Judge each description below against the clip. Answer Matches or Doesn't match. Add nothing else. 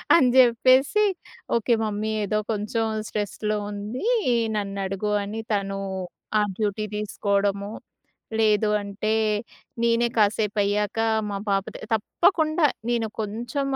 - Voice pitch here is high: Matches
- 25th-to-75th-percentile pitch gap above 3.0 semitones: Doesn't match